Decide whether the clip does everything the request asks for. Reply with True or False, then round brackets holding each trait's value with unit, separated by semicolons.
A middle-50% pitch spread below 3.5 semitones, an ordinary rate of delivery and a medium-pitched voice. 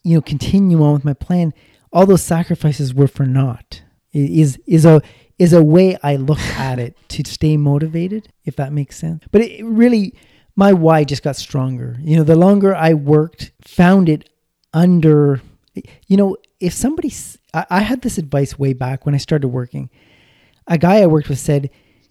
False (4.2 semitones; 180 wpm; 155 Hz)